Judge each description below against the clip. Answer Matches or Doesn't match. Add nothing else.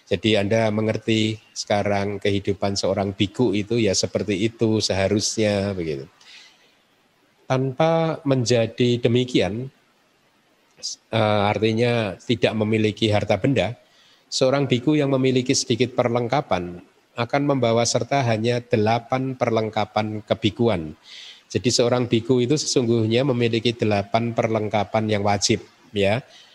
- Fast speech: Doesn't match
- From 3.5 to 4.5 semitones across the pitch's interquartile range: Doesn't match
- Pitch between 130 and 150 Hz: Doesn't match